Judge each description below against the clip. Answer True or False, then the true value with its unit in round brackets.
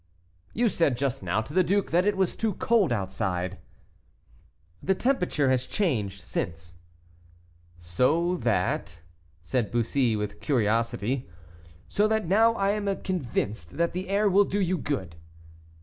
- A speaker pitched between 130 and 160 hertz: True (140 Hz)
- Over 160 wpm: False (145 wpm)